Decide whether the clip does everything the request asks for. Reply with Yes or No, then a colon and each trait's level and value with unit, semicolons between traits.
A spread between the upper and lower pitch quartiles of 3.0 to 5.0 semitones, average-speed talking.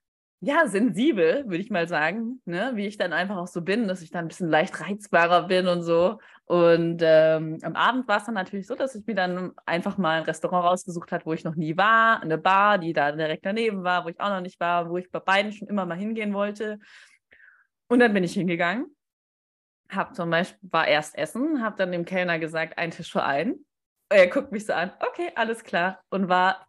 No: average, 4.0 semitones; fast, 225 wpm